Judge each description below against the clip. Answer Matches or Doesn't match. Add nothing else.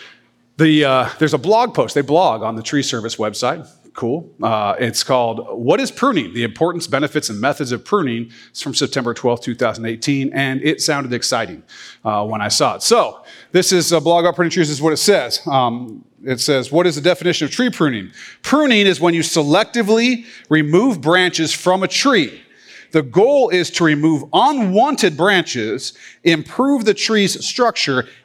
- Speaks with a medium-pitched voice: Matches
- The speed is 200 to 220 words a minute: Doesn't match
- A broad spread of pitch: Matches